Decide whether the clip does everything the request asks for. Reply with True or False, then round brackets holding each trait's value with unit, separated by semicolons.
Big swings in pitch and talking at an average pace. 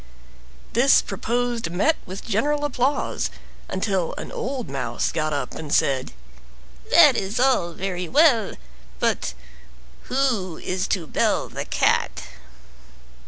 False (6.7 semitones; 115 wpm)